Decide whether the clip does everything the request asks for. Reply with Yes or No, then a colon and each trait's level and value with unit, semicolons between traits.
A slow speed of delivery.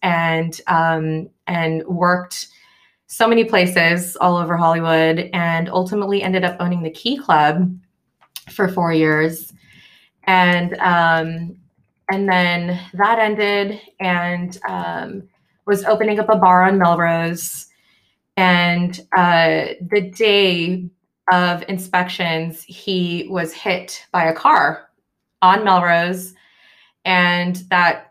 Yes: slow, 110 wpm